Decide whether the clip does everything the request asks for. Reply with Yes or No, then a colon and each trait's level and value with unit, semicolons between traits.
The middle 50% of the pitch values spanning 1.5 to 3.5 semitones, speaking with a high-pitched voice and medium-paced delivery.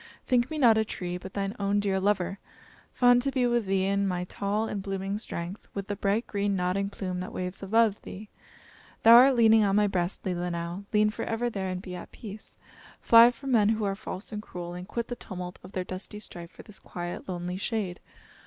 No: average, 3.1 semitones; high, 200 Hz; fast, 215 wpm